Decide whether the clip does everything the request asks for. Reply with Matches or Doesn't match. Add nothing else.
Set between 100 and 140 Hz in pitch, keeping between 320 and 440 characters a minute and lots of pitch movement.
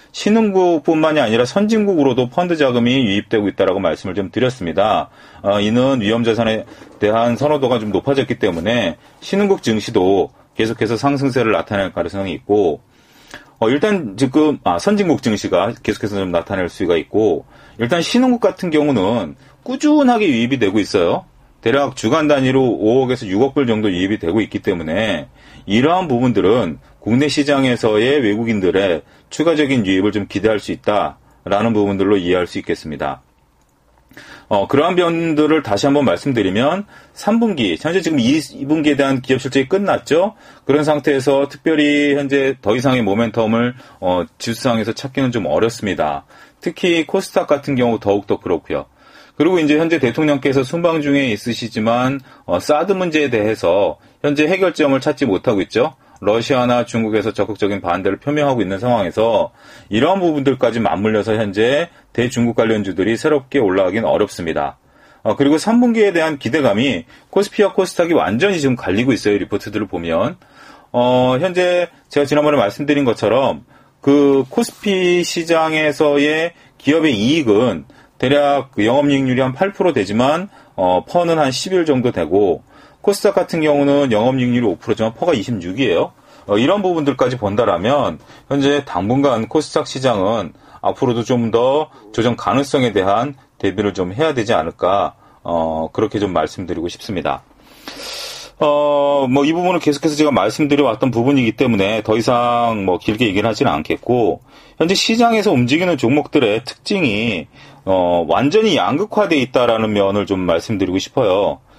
Matches